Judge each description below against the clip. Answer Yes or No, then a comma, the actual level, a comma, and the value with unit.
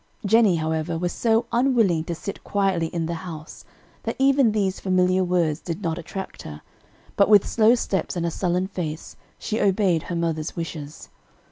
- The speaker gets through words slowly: No, average, 170 wpm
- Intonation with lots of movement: No, average, 3.7 semitones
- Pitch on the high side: No, medium, 180 Hz